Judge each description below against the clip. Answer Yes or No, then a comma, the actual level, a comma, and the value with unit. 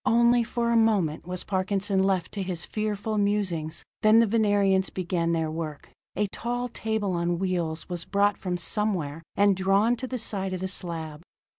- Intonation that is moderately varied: Yes, average, 3.6 semitones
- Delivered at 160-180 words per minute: Yes, average, 175 wpm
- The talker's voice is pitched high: Yes, high, 195 Hz